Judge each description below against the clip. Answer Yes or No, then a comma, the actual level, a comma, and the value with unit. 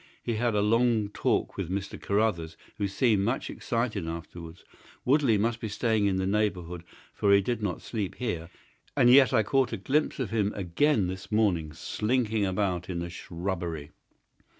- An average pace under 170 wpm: No, average, 175 wpm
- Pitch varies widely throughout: No, average, 4.3 semitones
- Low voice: Yes, low, 105 Hz